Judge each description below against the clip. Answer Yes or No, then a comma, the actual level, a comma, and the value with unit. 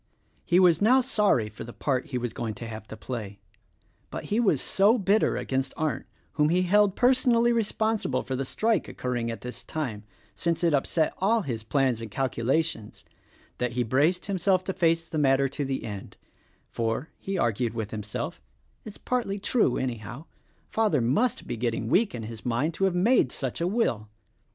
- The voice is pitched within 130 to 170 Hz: Yes, medium, 140 Hz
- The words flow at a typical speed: Yes, average, 190 wpm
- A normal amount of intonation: No, wide, 8.7 semitones